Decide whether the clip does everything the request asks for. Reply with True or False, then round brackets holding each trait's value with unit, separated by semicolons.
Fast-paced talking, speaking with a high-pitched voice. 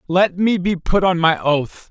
False (220 wpm; 175 Hz)